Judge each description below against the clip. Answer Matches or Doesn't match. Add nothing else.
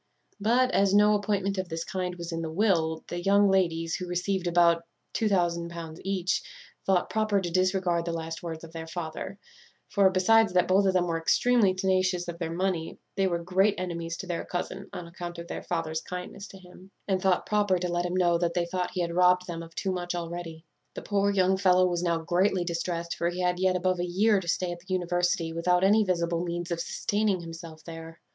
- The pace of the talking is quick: Matches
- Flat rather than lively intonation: Matches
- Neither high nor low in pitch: Matches